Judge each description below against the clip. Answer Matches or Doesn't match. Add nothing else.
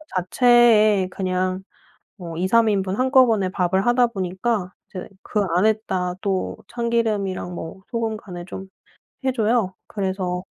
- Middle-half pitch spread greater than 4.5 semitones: Doesn't match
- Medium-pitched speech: Doesn't match